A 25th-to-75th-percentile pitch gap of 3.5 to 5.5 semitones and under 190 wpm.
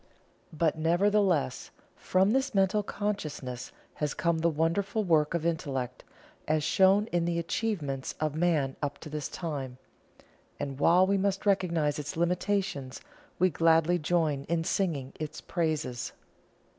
Yes: average, 4.1 semitones; slow, 135 wpm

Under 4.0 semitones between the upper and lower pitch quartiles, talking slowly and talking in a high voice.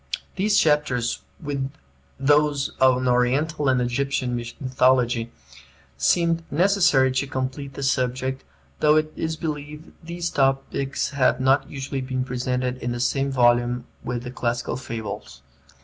No: average, 2.8 semitones; slow, 130 wpm; low, 135 Hz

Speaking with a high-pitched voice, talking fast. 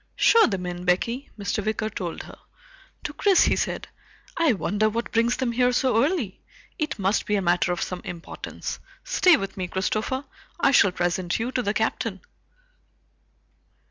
No: high, 215 Hz; average, 170 wpm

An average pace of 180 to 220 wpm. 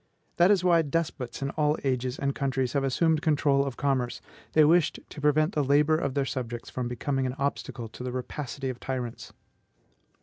Yes: average, 190 wpm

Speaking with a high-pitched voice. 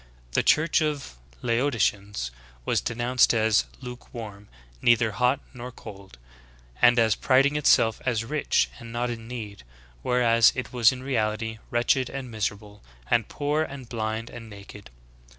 No: low, 115 Hz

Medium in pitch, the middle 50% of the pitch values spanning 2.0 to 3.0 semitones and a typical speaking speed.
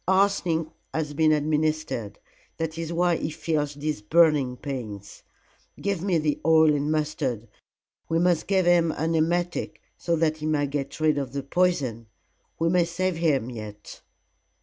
Yes: medium, 155 Hz; average, 2.7 semitones; average, 155 wpm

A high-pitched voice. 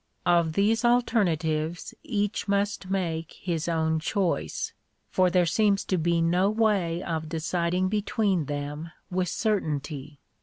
No: medium, 175 Hz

